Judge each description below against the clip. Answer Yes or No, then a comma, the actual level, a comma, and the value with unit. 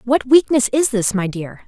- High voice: Yes, high, 235 Hz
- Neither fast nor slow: No, fast, 215 wpm